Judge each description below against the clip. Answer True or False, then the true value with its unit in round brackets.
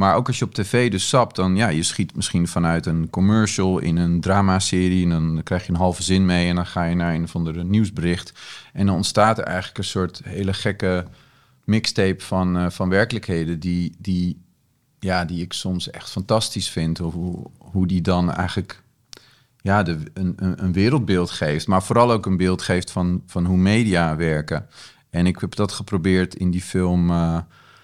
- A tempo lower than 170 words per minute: False (195 wpm)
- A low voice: True (90 Hz)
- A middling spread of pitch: False (2.2 semitones)